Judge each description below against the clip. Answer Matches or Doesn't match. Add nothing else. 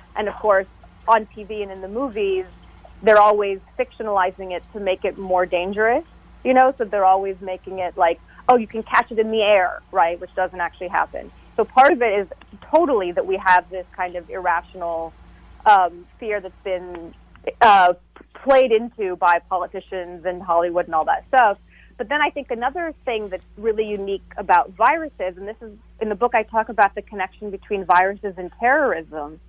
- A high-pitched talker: Matches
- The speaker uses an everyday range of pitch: Matches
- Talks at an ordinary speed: Matches